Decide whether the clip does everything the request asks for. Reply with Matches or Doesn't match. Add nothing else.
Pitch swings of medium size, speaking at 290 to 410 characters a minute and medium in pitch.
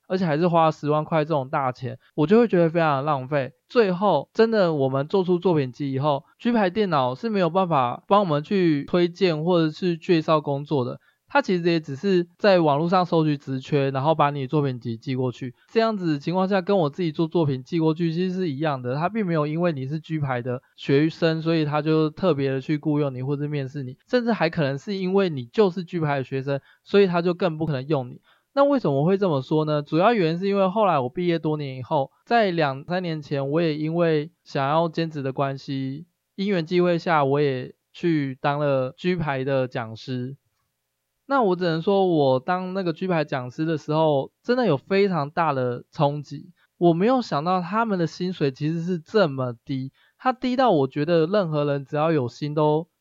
Matches